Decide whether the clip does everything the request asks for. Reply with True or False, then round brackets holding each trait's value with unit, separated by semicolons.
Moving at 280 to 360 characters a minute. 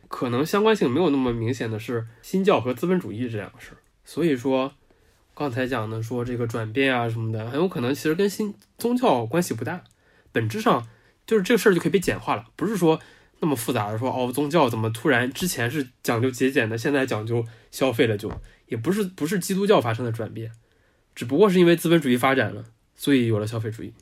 True (340 characters per minute)